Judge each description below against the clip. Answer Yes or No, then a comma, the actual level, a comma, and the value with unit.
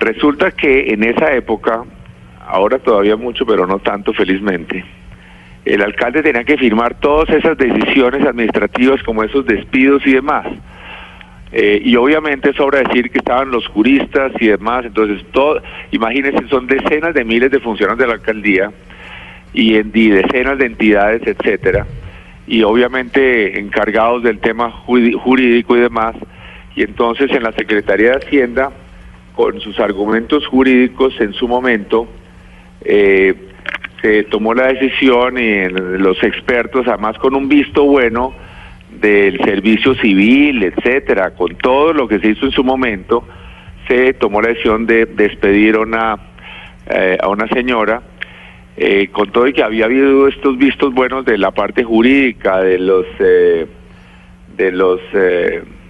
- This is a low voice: Yes, low, 120 Hz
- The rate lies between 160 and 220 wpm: No, average, 145 wpm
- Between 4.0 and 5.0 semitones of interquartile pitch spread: Yes, average, 4.3 semitones